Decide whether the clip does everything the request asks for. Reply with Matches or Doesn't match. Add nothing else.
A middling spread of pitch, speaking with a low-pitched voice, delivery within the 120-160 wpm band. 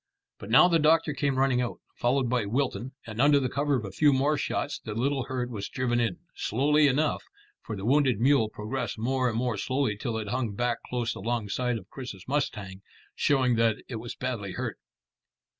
Doesn't match